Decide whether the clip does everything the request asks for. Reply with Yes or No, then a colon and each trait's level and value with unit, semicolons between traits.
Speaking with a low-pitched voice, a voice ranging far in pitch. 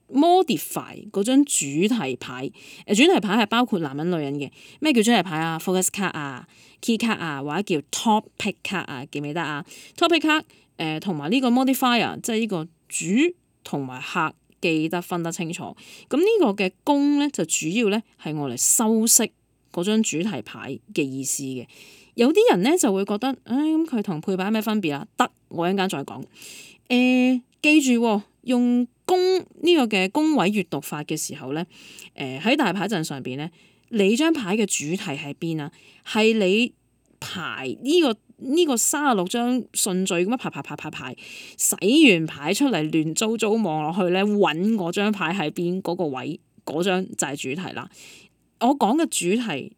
No: high, 200 Hz; wide, 7.4 semitones